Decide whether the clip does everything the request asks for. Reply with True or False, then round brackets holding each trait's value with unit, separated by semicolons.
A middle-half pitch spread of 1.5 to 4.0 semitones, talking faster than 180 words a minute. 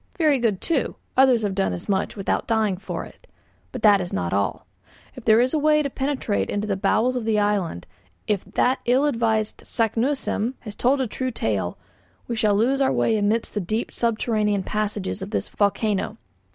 True (3.7 semitones; 195 wpm)